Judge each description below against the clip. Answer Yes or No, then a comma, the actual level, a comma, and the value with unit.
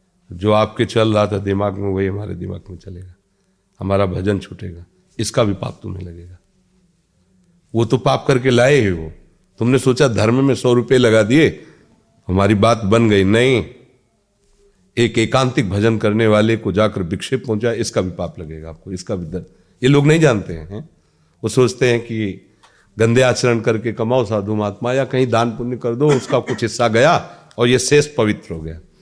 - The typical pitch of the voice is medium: No, low, 110 Hz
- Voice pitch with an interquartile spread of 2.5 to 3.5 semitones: No, average, 4.3 semitones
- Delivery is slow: No, average, 185 wpm